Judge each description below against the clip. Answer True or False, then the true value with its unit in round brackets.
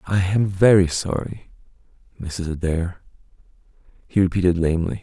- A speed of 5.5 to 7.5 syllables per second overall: False (5.0 syllables/s)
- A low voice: True (90 Hz)